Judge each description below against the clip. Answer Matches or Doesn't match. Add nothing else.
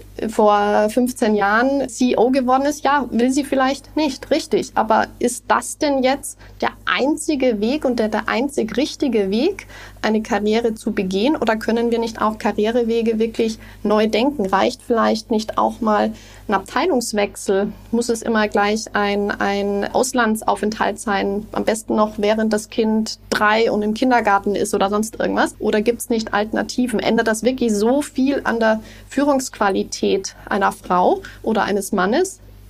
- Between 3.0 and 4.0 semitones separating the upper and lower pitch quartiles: Matches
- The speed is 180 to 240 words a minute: Doesn't match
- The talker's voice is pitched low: Doesn't match